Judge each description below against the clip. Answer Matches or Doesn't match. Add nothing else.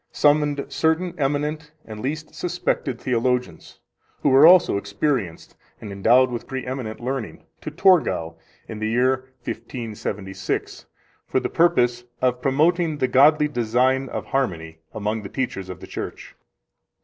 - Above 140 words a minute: Doesn't match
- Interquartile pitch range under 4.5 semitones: Doesn't match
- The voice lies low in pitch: Matches